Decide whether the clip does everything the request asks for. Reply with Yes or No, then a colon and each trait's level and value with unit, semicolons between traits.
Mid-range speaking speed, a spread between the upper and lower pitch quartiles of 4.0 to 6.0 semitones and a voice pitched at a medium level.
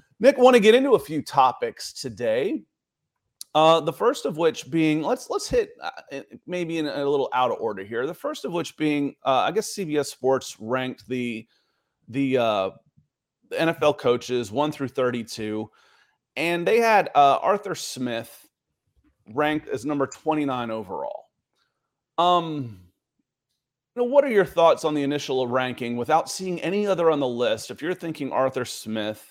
Yes: average, 165 wpm; average, 4.7 semitones; medium, 145 Hz